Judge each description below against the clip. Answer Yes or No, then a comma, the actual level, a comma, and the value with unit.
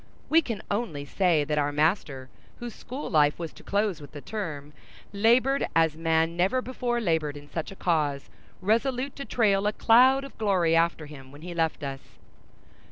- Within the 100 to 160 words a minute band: No, average, 180 wpm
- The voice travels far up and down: Yes, wide, 7.1 semitones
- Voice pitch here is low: No, medium, 170 Hz